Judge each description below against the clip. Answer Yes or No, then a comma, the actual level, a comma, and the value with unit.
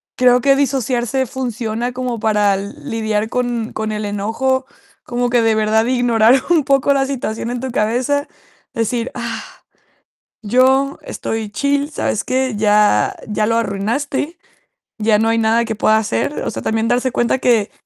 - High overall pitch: Yes, high, 235 Hz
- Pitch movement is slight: No, average, 3.1 semitones